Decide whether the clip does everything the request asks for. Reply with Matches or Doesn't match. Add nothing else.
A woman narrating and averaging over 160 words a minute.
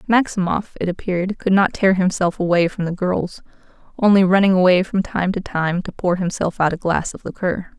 Matches